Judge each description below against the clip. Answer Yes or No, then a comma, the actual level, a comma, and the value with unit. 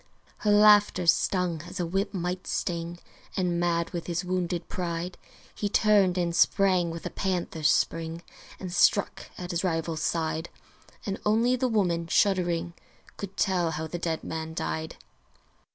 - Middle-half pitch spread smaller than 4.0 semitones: Yes, narrow, 2.4 semitones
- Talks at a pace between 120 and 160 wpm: Yes, average, 150 wpm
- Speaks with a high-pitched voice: No, medium, 175 Hz